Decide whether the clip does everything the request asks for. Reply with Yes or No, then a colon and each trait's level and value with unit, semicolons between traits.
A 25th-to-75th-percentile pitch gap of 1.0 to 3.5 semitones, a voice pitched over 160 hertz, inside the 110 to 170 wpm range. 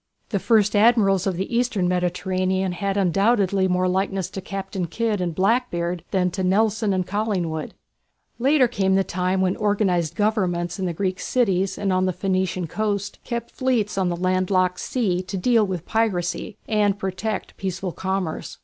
Yes: narrow, 2.4 semitones; high, 190 Hz; average, 165 wpm